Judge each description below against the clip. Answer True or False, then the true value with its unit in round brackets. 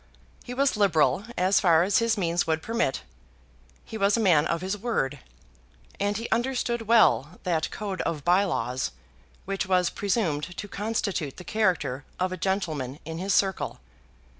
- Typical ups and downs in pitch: True (4.6 semitones)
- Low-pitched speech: False (185 Hz)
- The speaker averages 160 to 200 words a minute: True (165 wpm)